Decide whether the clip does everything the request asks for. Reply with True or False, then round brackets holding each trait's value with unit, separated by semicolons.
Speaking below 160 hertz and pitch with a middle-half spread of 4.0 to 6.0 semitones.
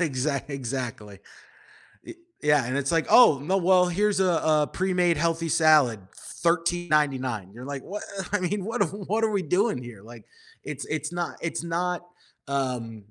False (165 Hz; 5.5 semitones)